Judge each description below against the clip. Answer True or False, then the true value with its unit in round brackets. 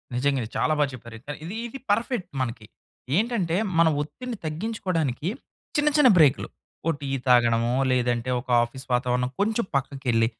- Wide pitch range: True (8.1 semitones)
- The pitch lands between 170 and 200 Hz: False (140 Hz)